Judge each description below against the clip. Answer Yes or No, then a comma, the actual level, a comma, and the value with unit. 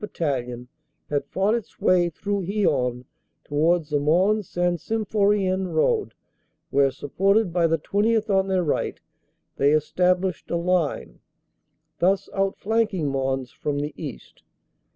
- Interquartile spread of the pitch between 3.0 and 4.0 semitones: No, average, 5.2 semitones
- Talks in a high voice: No, medium, 175 Hz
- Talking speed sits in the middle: No, slow, 130 wpm